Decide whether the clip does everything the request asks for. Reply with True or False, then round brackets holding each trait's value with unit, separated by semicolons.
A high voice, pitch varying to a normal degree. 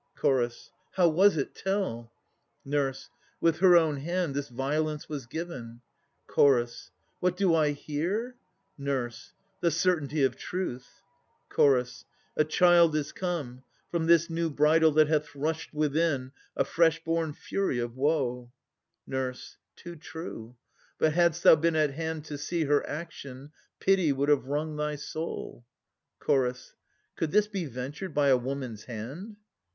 False (150 Hz; 3.8 semitones)